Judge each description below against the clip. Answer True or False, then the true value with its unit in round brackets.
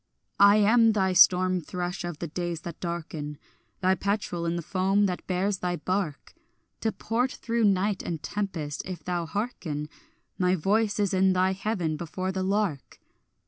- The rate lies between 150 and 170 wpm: True (165 wpm)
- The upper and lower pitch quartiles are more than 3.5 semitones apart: False (2.8 semitones)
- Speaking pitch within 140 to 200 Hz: True (185 Hz)